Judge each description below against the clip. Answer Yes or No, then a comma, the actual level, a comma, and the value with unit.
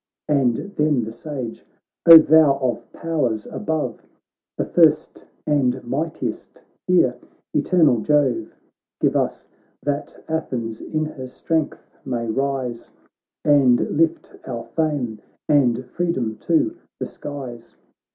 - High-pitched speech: No, medium, 140 Hz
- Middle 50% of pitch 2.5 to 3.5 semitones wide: No, average, 4.3 semitones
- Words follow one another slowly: Yes, slow, 115 wpm